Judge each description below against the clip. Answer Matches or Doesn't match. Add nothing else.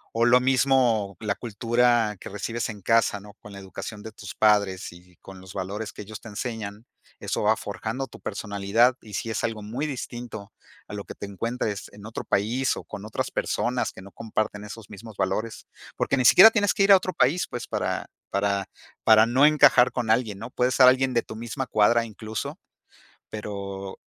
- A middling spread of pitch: Matches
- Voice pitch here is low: Matches